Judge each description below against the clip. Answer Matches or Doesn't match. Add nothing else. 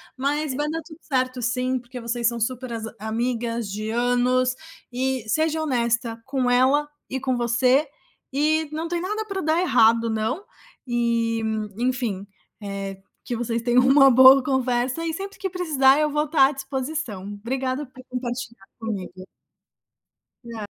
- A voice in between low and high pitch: Doesn't match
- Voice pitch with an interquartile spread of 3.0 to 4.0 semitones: Matches